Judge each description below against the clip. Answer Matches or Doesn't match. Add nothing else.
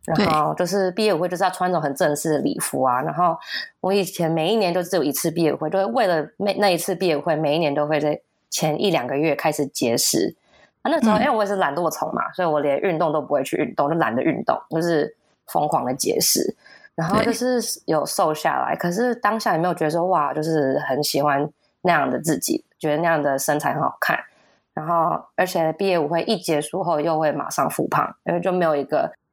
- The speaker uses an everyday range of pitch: Matches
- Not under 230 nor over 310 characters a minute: Doesn't match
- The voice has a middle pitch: Matches